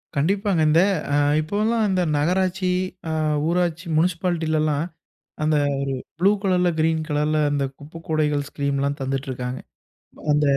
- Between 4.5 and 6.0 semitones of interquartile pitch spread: No, average, 3.7 semitones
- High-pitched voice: No, medium, 160 Hz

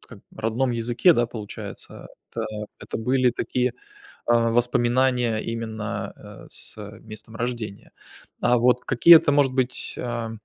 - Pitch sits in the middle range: No, low, 120 Hz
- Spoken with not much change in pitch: Yes, narrow, 1.8 semitones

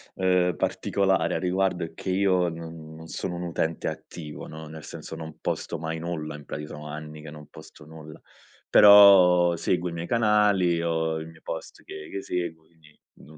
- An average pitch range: No, narrow, 2.3 semitones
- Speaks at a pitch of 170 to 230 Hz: No, very low, 80 Hz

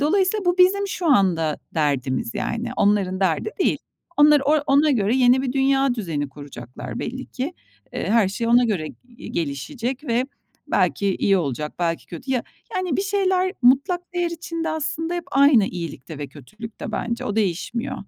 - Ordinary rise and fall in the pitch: No, wide, 8.8 semitones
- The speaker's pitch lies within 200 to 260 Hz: Yes, high, 245 Hz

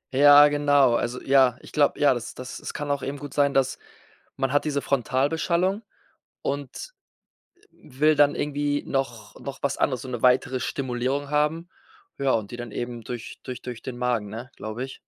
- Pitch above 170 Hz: No, low, 135 Hz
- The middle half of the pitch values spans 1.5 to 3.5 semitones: Yes, narrow, 2.6 semitones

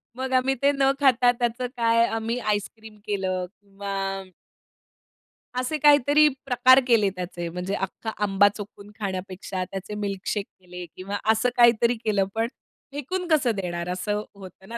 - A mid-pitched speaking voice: No, high, 210 Hz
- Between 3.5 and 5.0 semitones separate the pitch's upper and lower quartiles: Yes, average, 4.2 semitones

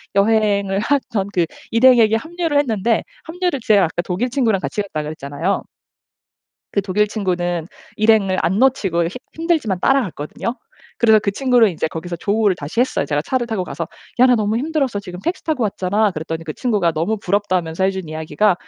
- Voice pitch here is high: Yes, high, 205 Hz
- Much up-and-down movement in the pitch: No, average, 5.0 semitones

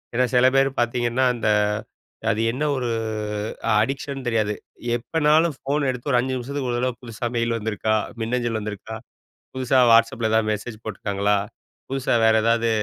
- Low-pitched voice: Yes, low, 120 Hz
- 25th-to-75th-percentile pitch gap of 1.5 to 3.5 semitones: Yes, average, 2.8 semitones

